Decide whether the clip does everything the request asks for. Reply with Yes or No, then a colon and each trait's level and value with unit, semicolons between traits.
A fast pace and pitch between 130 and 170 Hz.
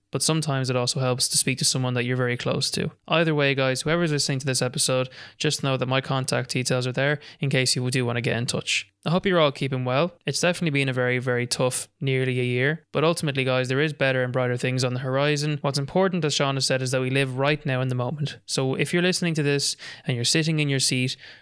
Yes: fast, 265 wpm; low, 135 Hz